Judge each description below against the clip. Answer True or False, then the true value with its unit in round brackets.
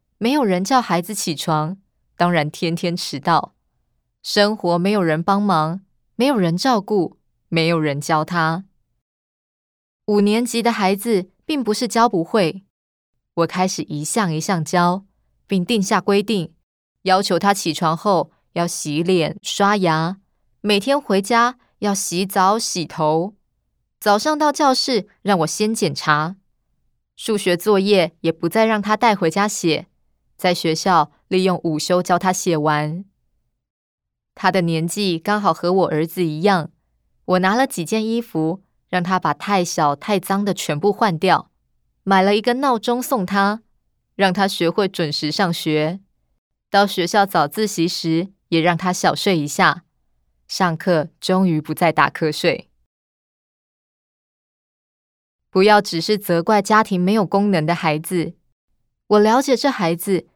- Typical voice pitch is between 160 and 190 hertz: True (185 Hz)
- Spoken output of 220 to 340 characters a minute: False (200 characters per minute)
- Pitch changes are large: False (3.8 semitones)